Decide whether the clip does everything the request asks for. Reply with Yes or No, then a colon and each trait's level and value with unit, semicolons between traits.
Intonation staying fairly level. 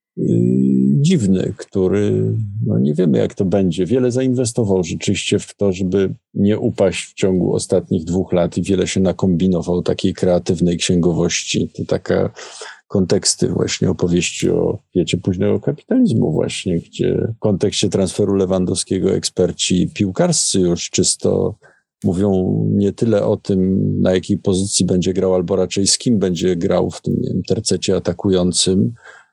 Yes: narrow, 2.0 semitones